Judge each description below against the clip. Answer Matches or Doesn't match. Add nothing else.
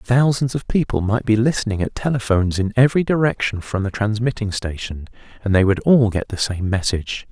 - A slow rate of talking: Doesn't match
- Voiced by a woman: Doesn't match